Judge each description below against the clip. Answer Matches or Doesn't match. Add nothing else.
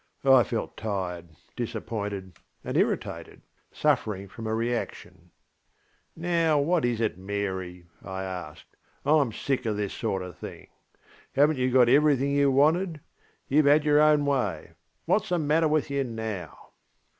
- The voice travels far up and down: Matches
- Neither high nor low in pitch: Doesn't match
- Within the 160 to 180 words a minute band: Doesn't match